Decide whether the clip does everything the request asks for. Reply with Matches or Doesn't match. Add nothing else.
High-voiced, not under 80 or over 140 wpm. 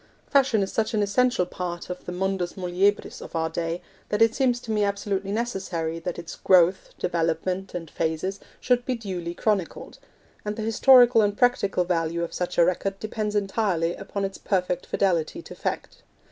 Doesn't match